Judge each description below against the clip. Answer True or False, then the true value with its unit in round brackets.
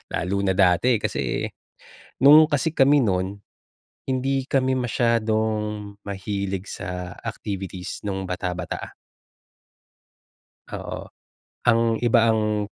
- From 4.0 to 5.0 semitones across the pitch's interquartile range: True (4.3 semitones)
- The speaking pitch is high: False (105 Hz)